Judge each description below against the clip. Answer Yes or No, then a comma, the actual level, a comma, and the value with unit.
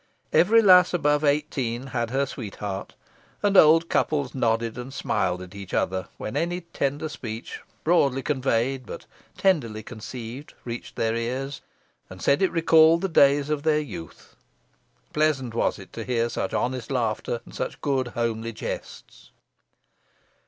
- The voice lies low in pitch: Yes, low, 130 Hz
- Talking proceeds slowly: No, average, 145 wpm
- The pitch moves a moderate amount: Yes, average, 4.8 semitones